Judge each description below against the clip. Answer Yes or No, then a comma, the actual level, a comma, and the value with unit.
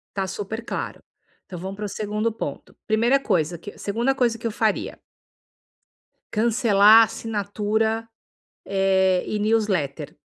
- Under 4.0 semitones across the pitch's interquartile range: Yes, narrow, 2.6 semitones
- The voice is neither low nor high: No, high, 210 Hz